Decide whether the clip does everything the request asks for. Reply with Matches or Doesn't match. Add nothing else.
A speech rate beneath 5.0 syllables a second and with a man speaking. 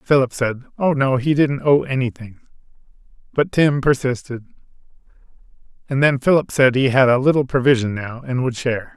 Doesn't match